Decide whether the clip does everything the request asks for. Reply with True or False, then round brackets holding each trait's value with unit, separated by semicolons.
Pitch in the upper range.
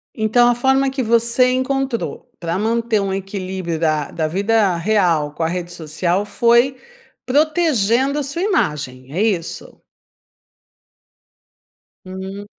True (210 Hz)